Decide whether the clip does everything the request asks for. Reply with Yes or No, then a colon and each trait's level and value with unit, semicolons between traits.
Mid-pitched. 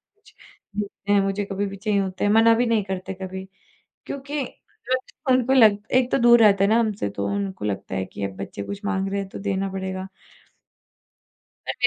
No: high, 200 Hz